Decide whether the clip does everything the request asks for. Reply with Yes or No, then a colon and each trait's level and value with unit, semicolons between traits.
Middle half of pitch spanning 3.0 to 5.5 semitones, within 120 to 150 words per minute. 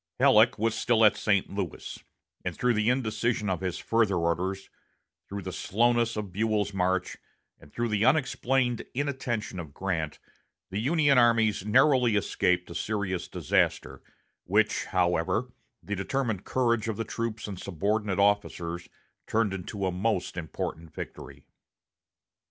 Yes: average, 3.8 semitones; average, 140 wpm